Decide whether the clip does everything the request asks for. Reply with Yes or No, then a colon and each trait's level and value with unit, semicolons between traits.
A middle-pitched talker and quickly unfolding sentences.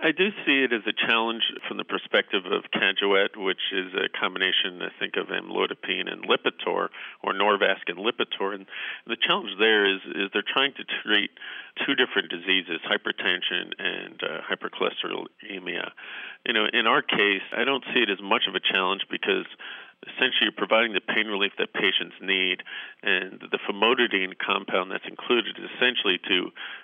No: medium, 160 Hz; average, 170 wpm